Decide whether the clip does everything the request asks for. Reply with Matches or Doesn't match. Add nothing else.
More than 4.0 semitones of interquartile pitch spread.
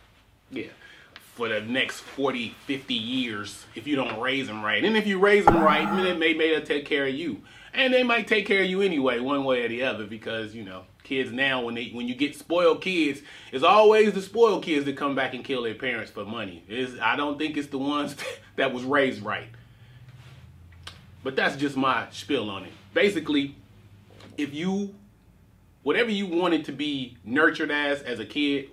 Matches